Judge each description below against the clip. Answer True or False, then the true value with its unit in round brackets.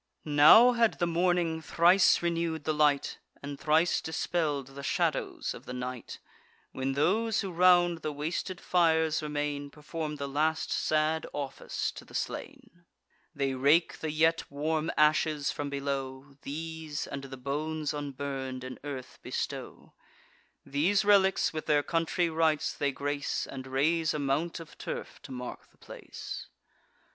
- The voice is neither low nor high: True (155 Hz)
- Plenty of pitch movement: False (2.8 semitones)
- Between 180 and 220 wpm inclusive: False (145 wpm)